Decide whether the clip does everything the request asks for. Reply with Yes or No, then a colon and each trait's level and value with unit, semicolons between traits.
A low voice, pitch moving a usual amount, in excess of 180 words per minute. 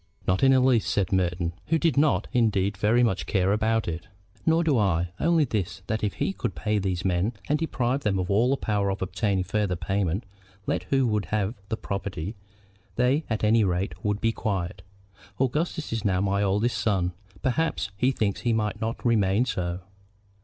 Yes: low, 105 Hz; average, 4.0 semitones; average, 190 wpm